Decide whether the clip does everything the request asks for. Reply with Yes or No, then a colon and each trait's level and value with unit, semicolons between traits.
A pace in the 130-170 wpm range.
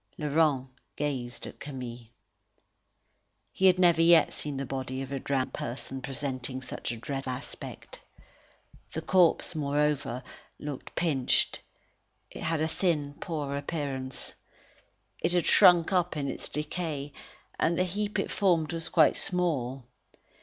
Yes: slow, 135 wpm